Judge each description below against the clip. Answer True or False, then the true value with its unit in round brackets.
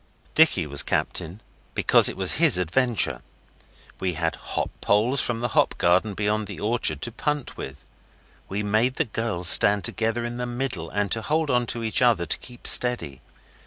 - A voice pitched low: True (110 Hz)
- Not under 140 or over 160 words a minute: False (175 wpm)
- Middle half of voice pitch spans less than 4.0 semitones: False (5.1 semitones)